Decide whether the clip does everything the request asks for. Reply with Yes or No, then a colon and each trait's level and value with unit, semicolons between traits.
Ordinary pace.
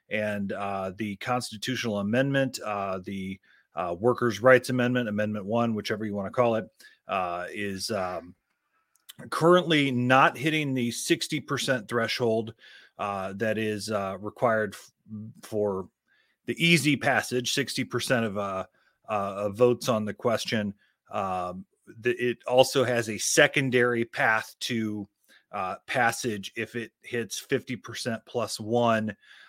No: slow, 130 wpm